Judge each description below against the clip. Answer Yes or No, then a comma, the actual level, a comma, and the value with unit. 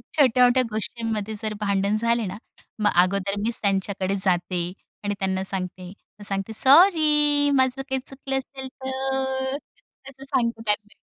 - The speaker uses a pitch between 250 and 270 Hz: No, high, 230 Hz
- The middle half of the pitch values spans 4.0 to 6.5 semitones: Yes, average, 5.1 semitones